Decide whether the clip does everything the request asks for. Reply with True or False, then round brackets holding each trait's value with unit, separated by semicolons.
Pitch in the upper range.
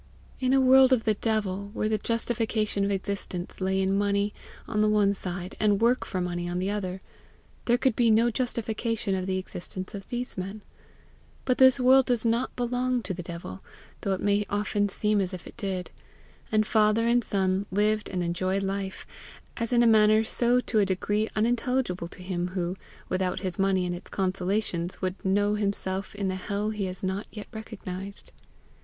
True (205 Hz)